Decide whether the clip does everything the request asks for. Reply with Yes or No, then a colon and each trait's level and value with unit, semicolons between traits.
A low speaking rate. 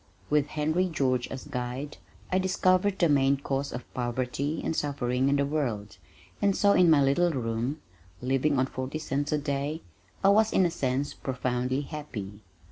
No: average, 170 wpm